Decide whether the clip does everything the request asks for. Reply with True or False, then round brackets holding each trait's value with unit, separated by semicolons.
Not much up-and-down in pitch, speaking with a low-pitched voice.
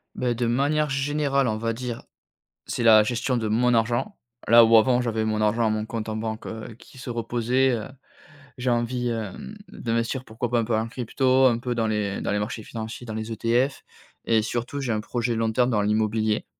True (2.1 semitones; 115 Hz)